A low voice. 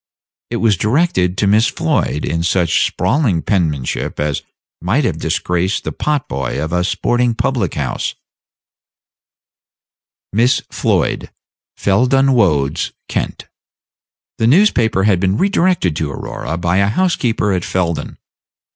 Yes: very low, 95 Hz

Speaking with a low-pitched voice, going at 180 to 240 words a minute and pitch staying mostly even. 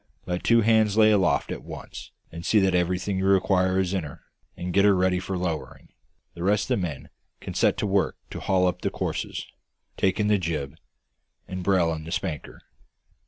Yes: very low, 95 Hz; fast, 205 wpm; narrow, 2.0 semitones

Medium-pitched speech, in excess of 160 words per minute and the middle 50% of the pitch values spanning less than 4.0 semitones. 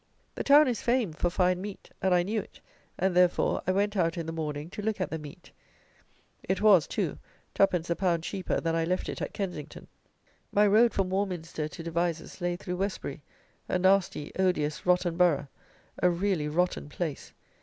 Yes: medium, 180 Hz; average, 185 wpm; average, 2.9 semitones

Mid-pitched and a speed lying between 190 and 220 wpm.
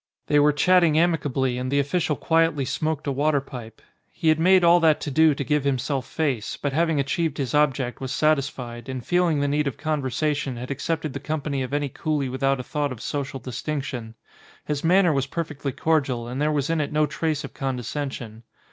Yes: medium, 145 Hz; average, 200 wpm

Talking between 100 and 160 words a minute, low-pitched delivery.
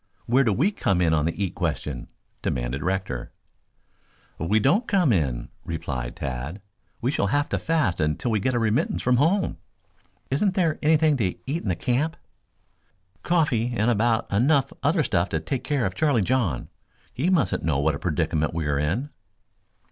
No: average, 175 wpm; low, 110 Hz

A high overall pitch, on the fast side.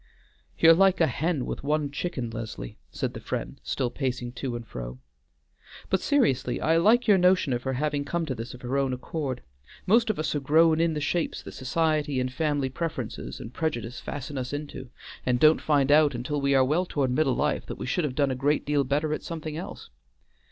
No: medium, 145 Hz; fast, 215 wpm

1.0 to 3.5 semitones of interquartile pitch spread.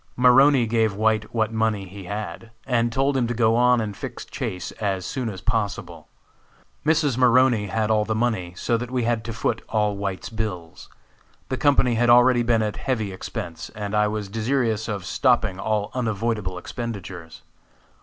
Yes: average, 2.8 semitones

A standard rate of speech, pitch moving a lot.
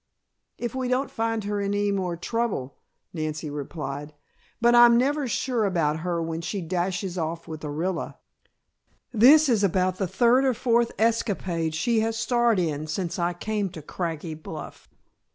Yes: average, 160 wpm; wide, 6.0 semitones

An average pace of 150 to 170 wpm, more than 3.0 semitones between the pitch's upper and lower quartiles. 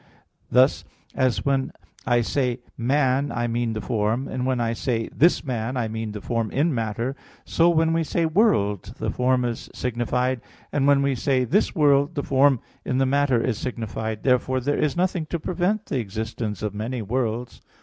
No: average, 185 wpm; average, 3.6 semitones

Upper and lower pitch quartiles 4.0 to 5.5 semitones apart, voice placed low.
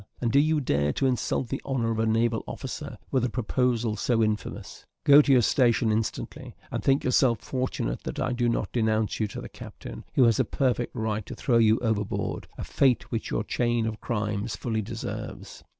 No: narrow, 2.6 semitones; low, 115 Hz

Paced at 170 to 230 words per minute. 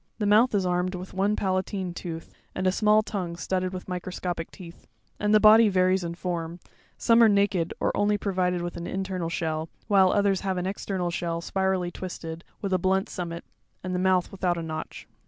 Yes: average, 195 wpm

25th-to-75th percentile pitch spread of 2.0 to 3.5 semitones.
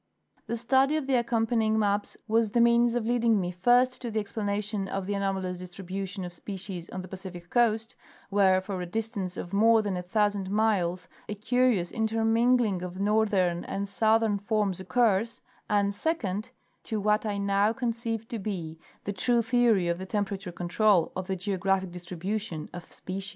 Yes: average, 3.2 semitones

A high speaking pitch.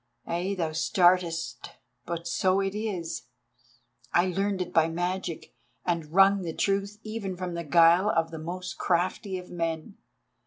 No: medium, 175 Hz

